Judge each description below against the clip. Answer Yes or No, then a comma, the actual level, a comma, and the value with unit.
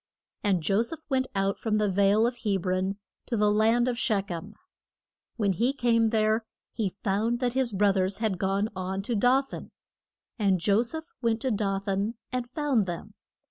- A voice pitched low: No, high, 215 Hz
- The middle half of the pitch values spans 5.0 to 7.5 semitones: No, average, 3.3 semitones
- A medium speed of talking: Yes, average, 190 wpm